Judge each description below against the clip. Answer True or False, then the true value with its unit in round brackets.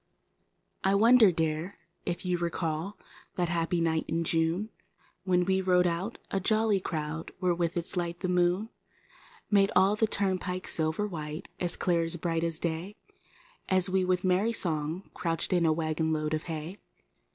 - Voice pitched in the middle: True (175 Hz)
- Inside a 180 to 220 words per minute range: False (170 wpm)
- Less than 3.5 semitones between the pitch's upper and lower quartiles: True (2.5 semitones)